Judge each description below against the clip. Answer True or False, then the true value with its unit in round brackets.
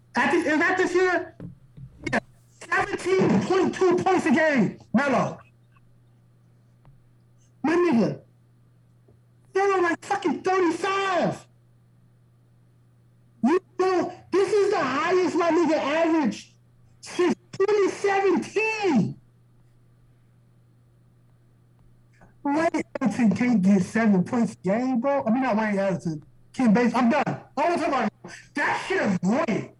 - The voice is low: False (220 Hz)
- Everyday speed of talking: False (115 wpm)